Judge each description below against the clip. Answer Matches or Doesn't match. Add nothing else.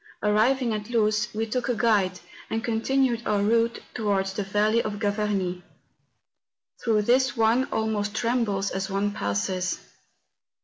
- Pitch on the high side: Matches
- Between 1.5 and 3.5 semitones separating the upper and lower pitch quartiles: Matches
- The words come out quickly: Doesn't match